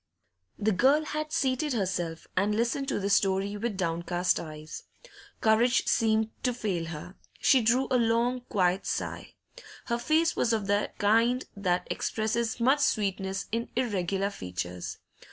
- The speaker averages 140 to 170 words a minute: Yes, average, 145 wpm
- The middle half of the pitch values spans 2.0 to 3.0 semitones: No, average, 4.5 semitones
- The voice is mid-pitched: No, high, 215 Hz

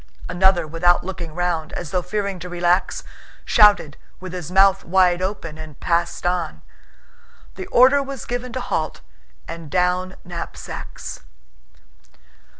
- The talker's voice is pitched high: No, medium, 180 Hz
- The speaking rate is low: Yes, slow, 130 wpm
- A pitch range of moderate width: No, narrow, 2.2 semitones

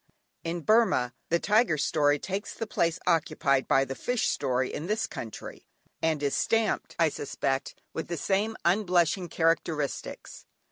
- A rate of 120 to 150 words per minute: Yes, average, 145 wpm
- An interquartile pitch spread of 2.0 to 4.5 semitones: No, average, 5.2 semitones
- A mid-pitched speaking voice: Yes, medium, 165 Hz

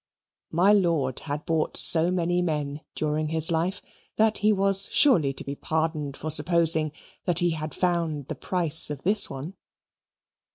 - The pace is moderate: Yes, average, 160 wpm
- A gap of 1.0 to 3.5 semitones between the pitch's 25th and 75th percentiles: Yes, average, 2.9 semitones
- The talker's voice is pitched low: No, medium, 160 Hz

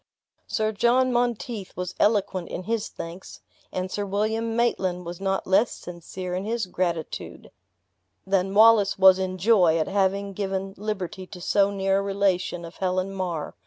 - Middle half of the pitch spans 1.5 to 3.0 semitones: Yes, narrow, 2.4 semitones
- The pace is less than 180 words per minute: Yes, average, 160 wpm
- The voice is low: No, high, 195 Hz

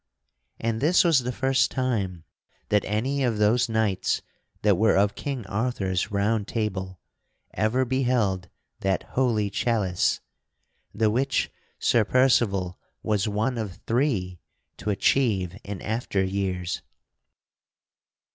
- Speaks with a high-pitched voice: No, low, 110 Hz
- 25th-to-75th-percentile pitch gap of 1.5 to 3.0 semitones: No, average, 4.2 semitones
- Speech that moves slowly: Yes, slow, 120 wpm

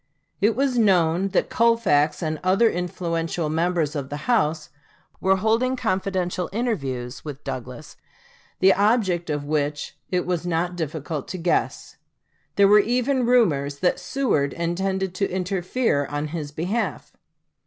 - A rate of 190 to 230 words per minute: No, slow, 135 wpm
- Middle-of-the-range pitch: Yes, medium, 180 Hz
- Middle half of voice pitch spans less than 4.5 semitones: No, average, 4.9 semitones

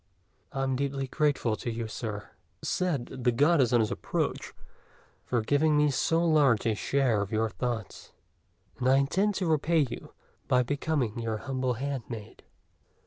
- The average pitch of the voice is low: Yes, low, 130 Hz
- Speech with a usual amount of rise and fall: Yes, average, 4.0 semitones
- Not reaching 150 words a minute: No, average, 155 wpm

